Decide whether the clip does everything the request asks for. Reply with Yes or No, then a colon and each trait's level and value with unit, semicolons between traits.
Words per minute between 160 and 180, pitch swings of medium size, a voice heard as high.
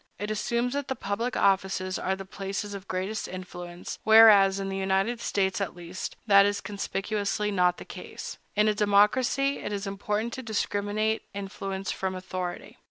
No: average, 165 wpm; narrow, 1.9 semitones; high, 200 Hz